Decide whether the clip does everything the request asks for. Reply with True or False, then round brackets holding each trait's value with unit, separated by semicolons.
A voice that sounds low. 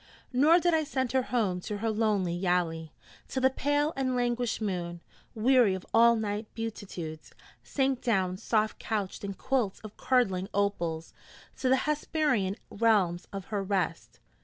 False (215 Hz)